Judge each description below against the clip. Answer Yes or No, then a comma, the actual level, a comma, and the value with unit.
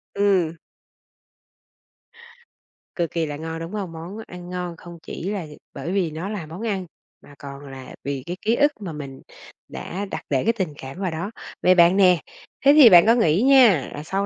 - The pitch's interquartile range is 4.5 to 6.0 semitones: No, average, 3.9 semitones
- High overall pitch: No, medium, 175 Hz